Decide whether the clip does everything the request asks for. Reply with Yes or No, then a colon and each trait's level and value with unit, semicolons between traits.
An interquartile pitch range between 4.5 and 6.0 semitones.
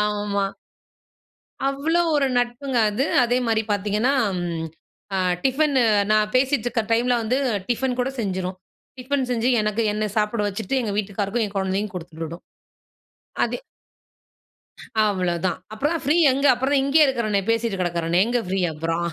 Yes: average, 4.9 semitones